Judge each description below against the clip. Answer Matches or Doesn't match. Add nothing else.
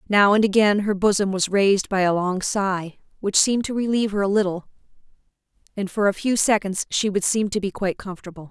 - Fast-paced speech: Matches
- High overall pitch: Matches